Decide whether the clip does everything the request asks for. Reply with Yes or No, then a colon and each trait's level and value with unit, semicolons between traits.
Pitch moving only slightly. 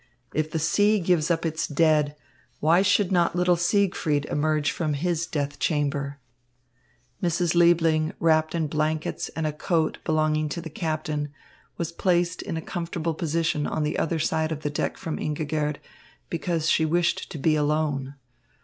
Yes: narrow, 1.9 semitones